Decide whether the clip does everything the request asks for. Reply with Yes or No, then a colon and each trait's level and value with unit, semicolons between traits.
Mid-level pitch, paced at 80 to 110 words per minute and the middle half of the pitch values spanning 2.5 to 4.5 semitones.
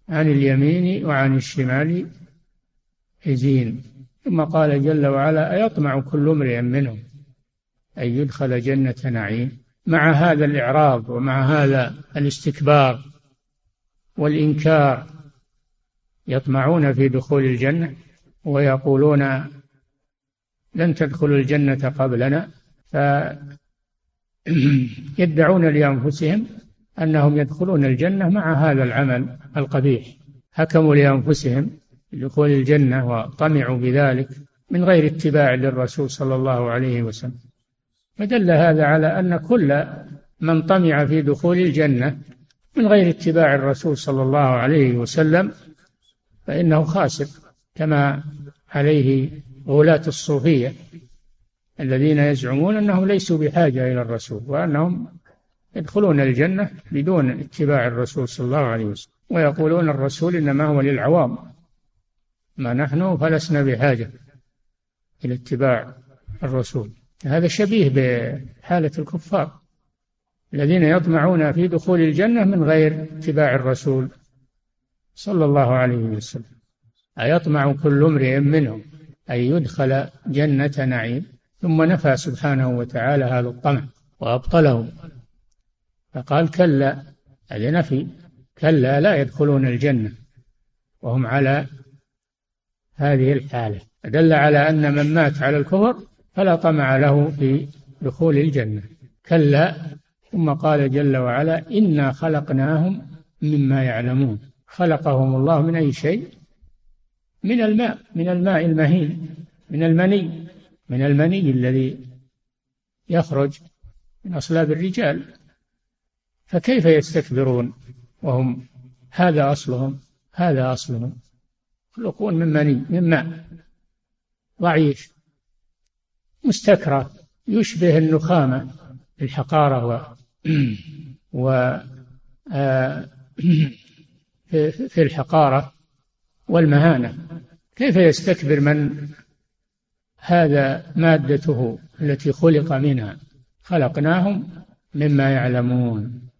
Yes: medium, 145 Hz; average, 95 wpm; average, 3.5 semitones